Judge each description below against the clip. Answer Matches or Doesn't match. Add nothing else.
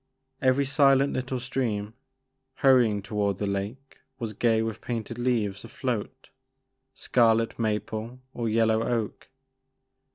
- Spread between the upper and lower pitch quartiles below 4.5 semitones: Matches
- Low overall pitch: Matches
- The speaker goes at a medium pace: Doesn't match